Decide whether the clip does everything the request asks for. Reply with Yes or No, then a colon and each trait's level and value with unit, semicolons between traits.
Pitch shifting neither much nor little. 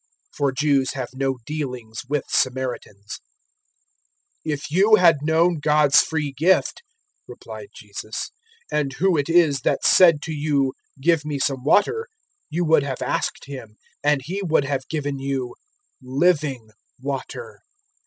Yes: average, 3.2 semitones